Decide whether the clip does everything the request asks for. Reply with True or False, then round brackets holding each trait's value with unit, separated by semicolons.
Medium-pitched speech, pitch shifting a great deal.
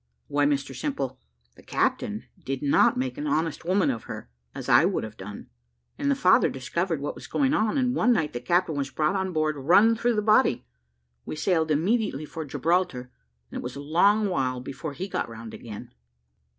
True (155 Hz; 6.3 semitones)